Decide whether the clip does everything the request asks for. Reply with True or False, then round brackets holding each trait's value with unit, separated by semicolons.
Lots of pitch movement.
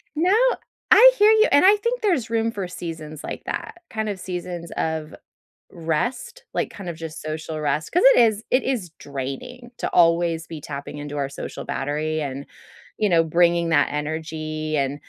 True (6.5 semitones)